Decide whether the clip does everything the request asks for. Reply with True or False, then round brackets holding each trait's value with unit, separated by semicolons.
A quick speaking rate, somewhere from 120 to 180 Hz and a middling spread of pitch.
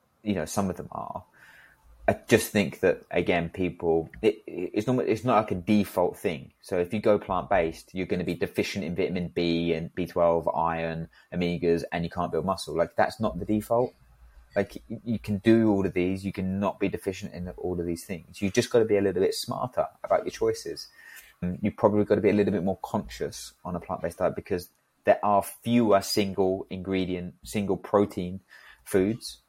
False (210 wpm; 95 Hz; 3.4 semitones)